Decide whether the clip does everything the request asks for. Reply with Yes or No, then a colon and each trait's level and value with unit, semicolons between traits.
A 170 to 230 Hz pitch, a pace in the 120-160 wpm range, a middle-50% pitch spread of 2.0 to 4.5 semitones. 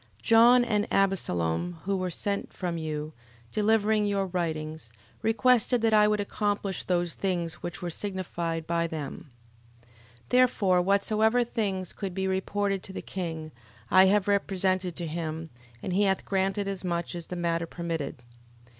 Yes: high, 190 Hz; average, 155 wpm; average, 3.3 semitones